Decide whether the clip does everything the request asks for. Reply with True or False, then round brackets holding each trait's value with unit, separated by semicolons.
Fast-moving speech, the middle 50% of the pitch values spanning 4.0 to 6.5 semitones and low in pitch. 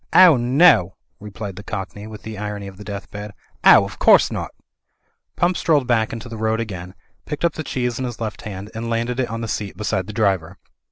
False (215 wpm; 3.1 semitones; 110 Hz)